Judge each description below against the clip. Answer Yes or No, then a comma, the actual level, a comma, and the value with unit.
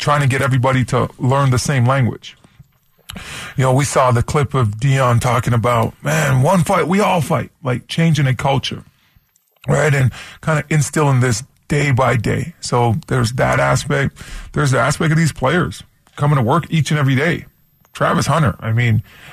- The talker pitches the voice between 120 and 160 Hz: Yes, low, 135 Hz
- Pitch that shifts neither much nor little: Yes, average, 3.6 semitones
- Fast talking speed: No, average, 185 wpm